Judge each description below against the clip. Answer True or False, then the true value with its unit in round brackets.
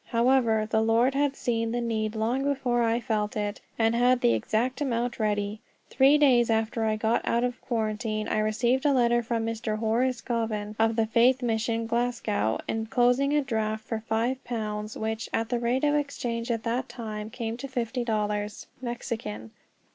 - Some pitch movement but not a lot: False (2.0 semitones)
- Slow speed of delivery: False (175 wpm)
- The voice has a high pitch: True (230 Hz)